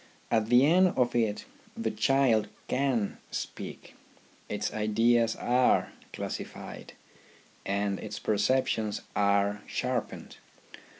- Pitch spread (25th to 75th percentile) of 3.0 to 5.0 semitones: Yes, average, 3.5 semitones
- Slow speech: Yes, slow, 100 wpm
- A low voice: Yes, low, 115 Hz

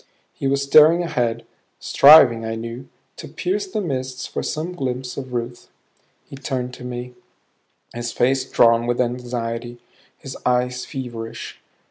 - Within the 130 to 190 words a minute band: Yes, average, 140 wpm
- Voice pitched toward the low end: Yes, low, 125 Hz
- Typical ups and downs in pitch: No, narrow, 2.3 semitones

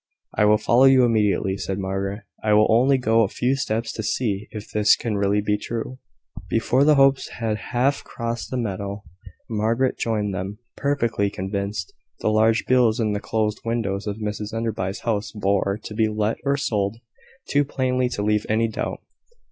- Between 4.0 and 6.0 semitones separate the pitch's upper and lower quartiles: No, narrow, 2.5 semitones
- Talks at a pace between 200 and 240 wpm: No, average, 180 wpm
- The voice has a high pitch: No, low, 110 Hz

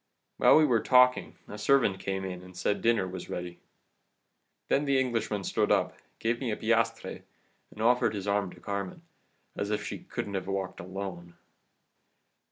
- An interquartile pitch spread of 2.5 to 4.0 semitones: Yes, average, 3.7 semitones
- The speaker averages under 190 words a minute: Yes, average, 170 wpm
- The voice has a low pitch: Yes, low, 100 Hz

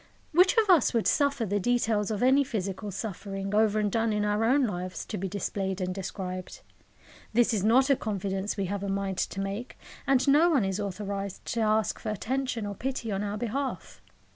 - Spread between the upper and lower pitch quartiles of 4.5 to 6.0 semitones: No, average, 3.7 semitones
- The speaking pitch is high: Yes, high, 210 Hz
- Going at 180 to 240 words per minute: Yes, average, 200 wpm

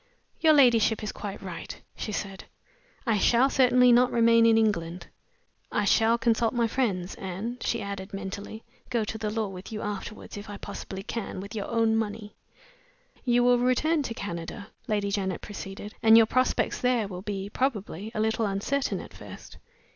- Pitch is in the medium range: No, high, 220 Hz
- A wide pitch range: No, average, 2.9 semitones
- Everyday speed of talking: Yes, average, 170 wpm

